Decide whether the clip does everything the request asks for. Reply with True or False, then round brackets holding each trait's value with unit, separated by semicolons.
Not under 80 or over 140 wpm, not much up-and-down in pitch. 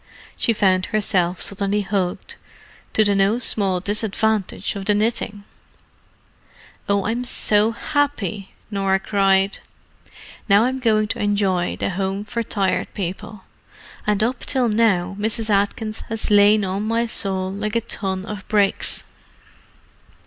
True (135 wpm; 2.1 semitones)